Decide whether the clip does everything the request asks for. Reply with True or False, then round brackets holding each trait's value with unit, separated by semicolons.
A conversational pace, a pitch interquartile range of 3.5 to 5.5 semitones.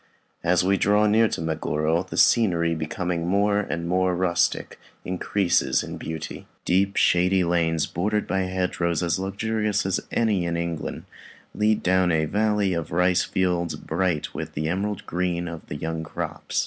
False (160 wpm; 2.7 semitones)